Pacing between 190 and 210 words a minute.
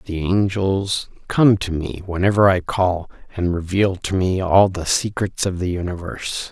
No: average, 165 wpm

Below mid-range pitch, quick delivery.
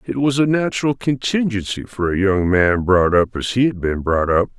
Yes: low, 105 Hz; fast, 220 wpm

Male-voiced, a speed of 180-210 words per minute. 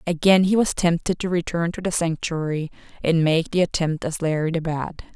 No: female; average, 200 wpm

